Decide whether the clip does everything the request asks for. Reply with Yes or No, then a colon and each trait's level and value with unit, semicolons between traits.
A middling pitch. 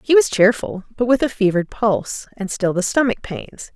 No: high, 215 Hz